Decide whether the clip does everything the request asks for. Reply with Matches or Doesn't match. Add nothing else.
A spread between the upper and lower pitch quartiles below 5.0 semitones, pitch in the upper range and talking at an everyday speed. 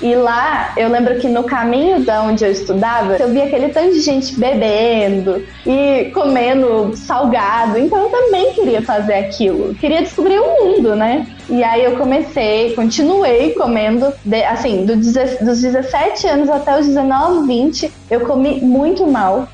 Matches